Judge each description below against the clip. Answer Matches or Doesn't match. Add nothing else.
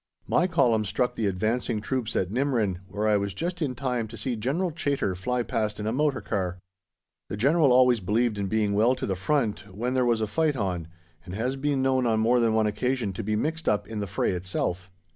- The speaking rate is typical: Doesn't match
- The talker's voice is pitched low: Matches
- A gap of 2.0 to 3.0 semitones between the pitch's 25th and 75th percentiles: Doesn't match